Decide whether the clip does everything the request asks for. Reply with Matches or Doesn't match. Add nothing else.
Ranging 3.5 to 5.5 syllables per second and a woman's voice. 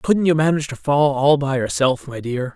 Doesn't match